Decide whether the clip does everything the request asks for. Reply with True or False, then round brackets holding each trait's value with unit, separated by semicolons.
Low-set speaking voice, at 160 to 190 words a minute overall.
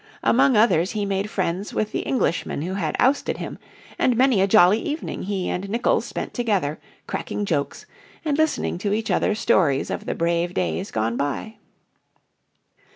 False (200 Hz; 165 wpm)